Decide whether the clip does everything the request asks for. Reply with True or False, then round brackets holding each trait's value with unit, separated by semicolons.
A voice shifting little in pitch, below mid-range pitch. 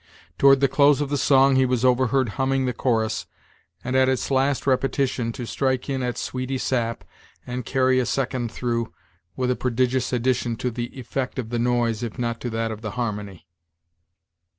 True (2.1 semitones; 125 Hz)